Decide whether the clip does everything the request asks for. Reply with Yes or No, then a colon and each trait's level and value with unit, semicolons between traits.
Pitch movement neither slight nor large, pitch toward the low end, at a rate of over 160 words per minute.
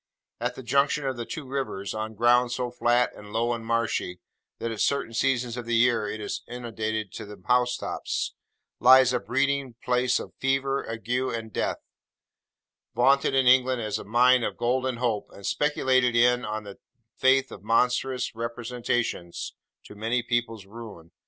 No: narrow, 2.1 semitones; low, 120 Hz; average, 170 wpm